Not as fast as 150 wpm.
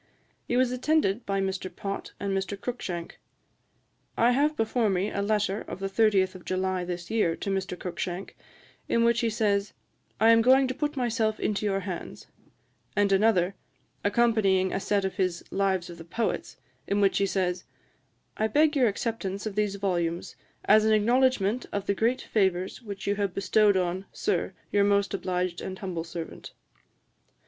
No: average, 175 wpm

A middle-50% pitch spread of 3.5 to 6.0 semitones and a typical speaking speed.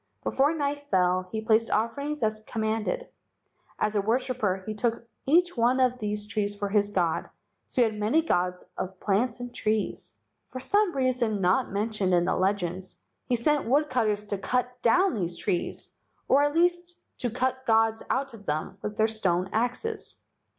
Yes: average, 4.2 semitones; average, 175 wpm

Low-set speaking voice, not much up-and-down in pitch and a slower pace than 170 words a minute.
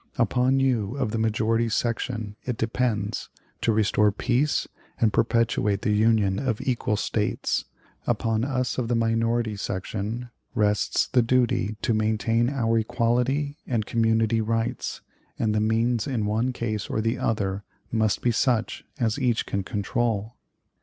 Yes: low, 115 Hz; narrow, 2.0 semitones; average, 145 wpm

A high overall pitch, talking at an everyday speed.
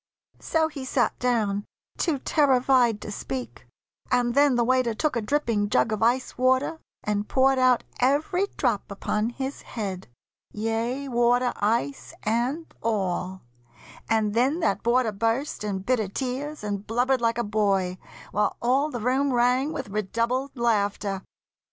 Yes: high, 240 Hz; average, 145 wpm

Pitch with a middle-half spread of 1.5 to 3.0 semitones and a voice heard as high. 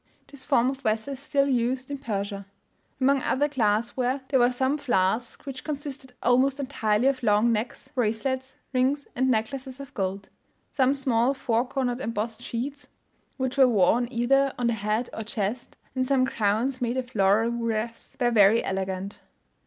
No: average, 3.4 semitones; high, 245 Hz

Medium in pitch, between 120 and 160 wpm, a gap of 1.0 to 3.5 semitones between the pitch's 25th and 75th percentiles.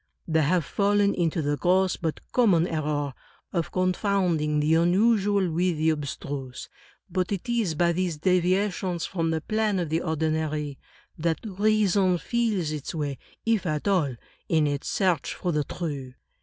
No: medium, 170 Hz; average, 155 wpm; average, 3.9 semitones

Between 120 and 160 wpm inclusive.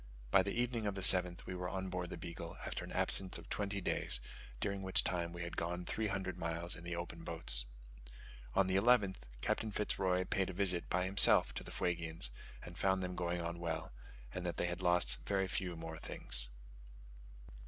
No: fast, 205 wpm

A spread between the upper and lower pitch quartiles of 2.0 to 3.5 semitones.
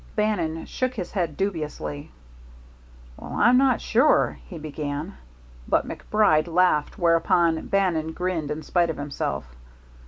No: average, 4.3 semitones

